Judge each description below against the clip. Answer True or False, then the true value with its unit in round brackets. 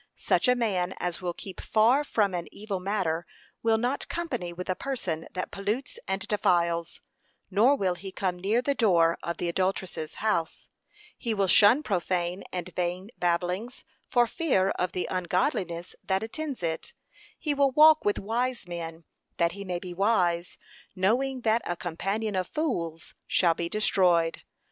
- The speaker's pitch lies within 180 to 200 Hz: True (190 Hz)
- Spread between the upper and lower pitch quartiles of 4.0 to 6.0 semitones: True (4.5 semitones)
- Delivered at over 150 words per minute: True (165 wpm)